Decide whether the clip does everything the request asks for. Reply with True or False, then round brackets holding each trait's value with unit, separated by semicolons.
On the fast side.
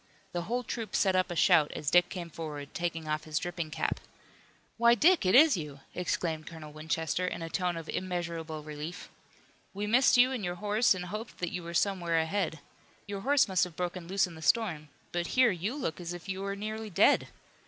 True (210 wpm)